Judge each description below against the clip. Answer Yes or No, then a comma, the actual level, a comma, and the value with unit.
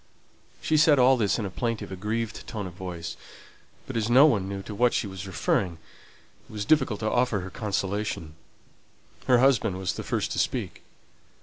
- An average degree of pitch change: Yes, average, 4.1 semitones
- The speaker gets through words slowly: No, average, 185 wpm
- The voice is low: Yes, low, 105 Hz